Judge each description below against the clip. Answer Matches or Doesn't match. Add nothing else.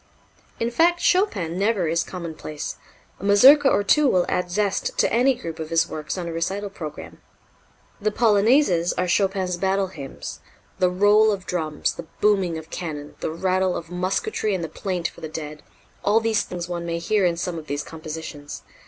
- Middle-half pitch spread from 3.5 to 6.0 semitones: Matches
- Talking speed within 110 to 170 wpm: Doesn't match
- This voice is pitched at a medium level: Matches